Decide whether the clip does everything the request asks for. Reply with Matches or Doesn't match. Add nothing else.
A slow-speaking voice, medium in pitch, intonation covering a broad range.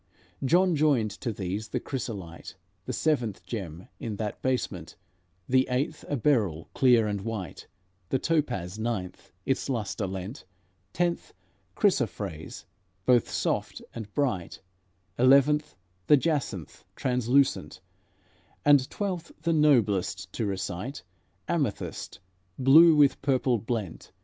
Doesn't match